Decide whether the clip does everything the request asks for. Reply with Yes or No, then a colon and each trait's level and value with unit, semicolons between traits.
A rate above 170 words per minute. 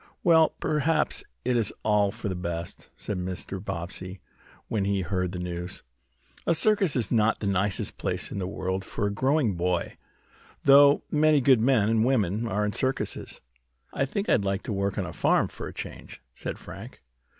Yes: average, 185 wpm